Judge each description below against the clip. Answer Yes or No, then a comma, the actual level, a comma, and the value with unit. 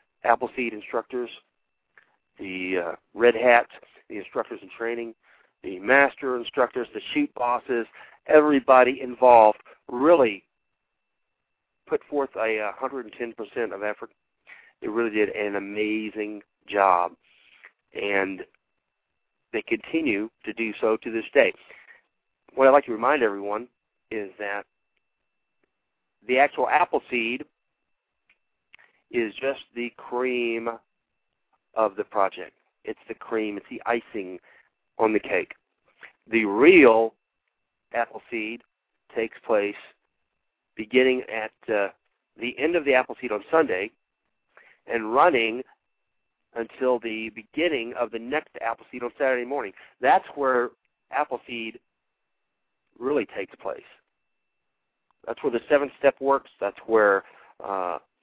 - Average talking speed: No, slow, 115 wpm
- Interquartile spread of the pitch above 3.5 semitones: No, average, 2.9 semitones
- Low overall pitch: Yes, low, 115 Hz